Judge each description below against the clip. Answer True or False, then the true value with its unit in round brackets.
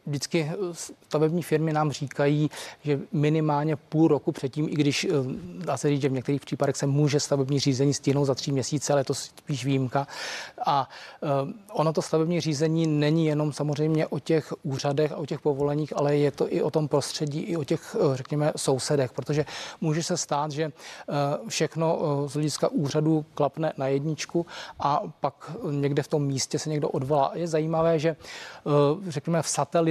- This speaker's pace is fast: True (175 wpm)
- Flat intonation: True (1.9 semitones)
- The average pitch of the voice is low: False (150 Hz)